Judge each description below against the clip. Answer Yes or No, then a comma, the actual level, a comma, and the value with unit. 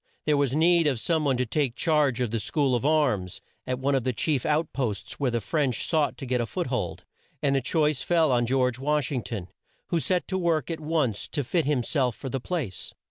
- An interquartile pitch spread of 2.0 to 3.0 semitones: No, average, 4.0 semitones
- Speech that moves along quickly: Yes, fast, 240 wpm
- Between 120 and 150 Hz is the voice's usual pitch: Yes, low, 135 Hz